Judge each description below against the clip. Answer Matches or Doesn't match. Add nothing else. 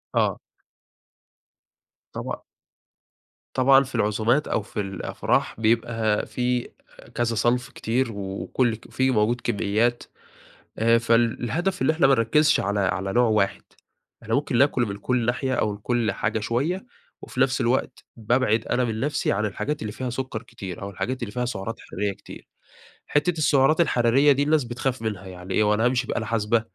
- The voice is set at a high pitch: Doesn't match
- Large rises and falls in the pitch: Doesn't match